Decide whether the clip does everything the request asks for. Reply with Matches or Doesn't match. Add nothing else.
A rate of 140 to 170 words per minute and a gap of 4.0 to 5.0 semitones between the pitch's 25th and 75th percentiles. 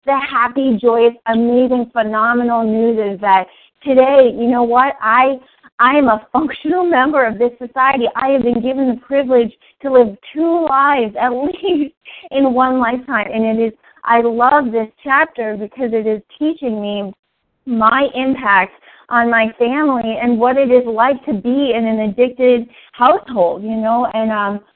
Doesn't match